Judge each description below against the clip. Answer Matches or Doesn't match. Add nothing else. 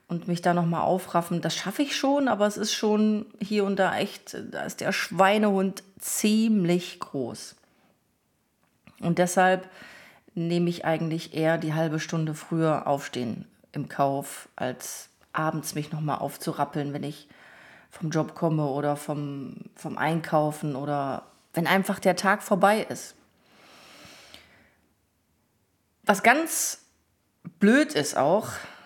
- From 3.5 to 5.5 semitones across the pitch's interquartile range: Matches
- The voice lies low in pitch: Doesn't match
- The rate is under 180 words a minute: Matches